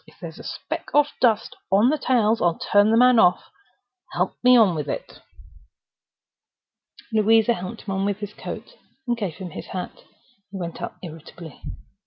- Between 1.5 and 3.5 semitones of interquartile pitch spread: No, average, 4.5 semitones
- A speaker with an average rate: Yes, average, 170 wpm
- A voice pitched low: No, high, 210 Hz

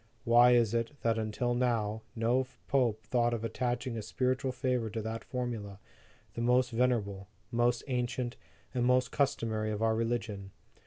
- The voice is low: Yes, low, 120 Hz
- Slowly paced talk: No, average, 155 wpm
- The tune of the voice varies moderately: No, narrow, 2.0 semitones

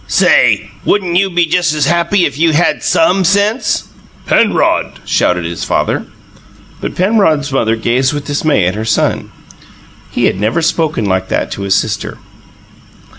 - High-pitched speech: No, medium, 155 Hz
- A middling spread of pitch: No, wide, 8.2 semitones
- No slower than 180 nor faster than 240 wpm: No, average, 160 wpm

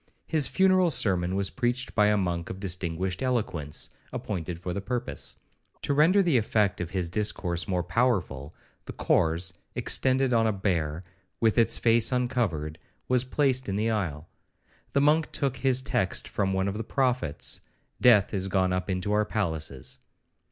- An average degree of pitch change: No, wide, 5.9 semitones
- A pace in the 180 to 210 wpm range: No, average, 160 wpm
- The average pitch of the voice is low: Yes, low, 105 Hz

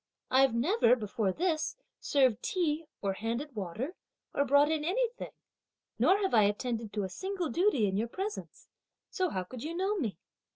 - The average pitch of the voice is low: No, very high, 280 Hz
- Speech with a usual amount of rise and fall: No, wide, 8.6 semitones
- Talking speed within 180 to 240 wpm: No, average, 170 wpm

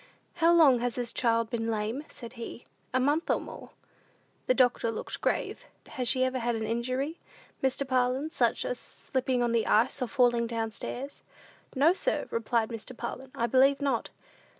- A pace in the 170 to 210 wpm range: Yes, average, 175 wpm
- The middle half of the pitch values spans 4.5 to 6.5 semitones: No, narrow, 2.5 semitones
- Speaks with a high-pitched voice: Yes, very high, 250 Hz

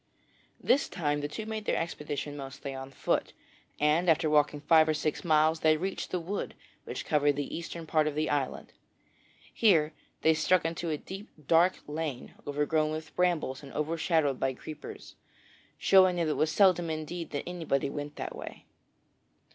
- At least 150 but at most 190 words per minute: Yes, average, 170 wpm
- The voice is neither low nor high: Yes, medium, 155 Hz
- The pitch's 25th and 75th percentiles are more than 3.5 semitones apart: No, narrow, 2.5 semitones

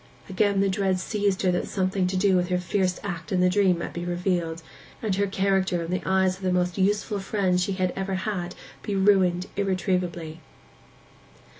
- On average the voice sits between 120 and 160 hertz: No, medium, 185 Hz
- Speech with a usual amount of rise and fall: No, narrow, 1.5 semitones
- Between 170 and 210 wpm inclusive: Yes, average, 190 wpm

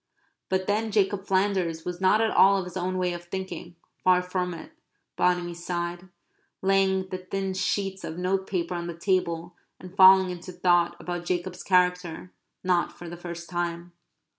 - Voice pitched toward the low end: No, medium, 180 Hz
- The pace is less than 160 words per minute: No, average, 165 wpm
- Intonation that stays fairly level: Yes, narrow, 1.5 semitones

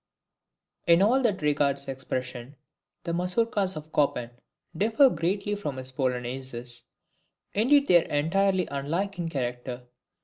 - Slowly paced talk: Yes, slow, 125 wpm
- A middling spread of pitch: No, wide, 7.0 semitones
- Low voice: No, medium, 155 Hz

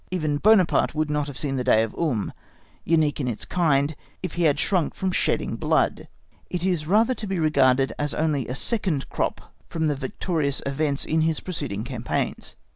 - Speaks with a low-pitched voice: No, medium, 150 Hz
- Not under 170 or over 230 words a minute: Yes, average, 190 wpm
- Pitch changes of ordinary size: Yes, average, 4.1 semitones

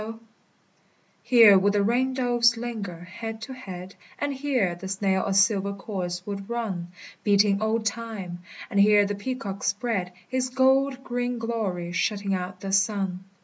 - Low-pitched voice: No, high, 205 Hz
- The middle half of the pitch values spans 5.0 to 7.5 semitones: No, average, 3.7 semitones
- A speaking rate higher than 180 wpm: No, average, 155 wpm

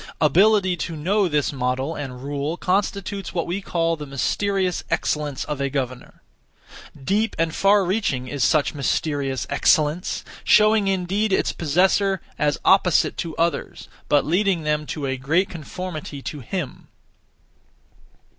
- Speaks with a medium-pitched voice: Yes, medium, 165 Hz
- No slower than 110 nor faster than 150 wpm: Yes, slow, 135 wpm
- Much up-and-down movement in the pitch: No, average, 4.9 semitones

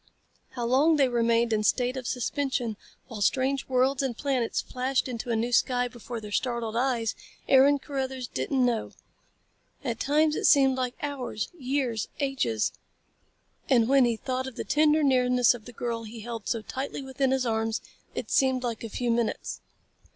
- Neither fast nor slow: Yes, average, 175 wpm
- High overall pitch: Yes, very high, 250 Hz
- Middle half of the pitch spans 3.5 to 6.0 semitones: No, narrow, 2.4 semitones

